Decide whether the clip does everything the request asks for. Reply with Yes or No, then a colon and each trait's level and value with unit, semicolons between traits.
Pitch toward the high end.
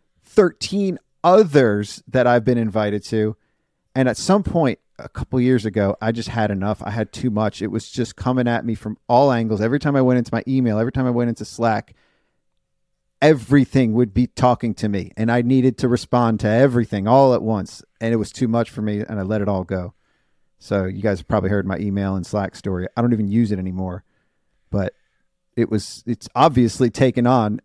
No: low, 115 Hz